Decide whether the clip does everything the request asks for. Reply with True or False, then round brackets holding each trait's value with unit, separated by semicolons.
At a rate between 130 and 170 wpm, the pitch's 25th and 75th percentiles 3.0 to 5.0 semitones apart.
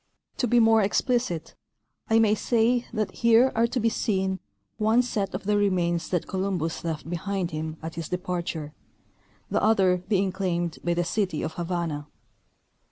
True (165 wpm; 4.5 semitones)